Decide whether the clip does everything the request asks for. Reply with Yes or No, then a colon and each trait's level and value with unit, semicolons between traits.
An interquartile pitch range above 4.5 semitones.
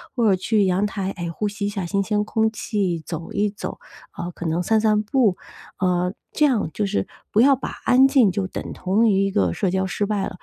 No: average, 2.8 semitones